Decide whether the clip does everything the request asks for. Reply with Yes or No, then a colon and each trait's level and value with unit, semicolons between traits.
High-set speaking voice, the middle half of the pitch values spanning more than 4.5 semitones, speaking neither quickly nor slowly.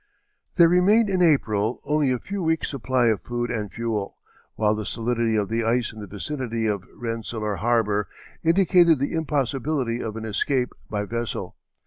No: low, 120 Hz; average, 5.3 semitones; average, 165 wpm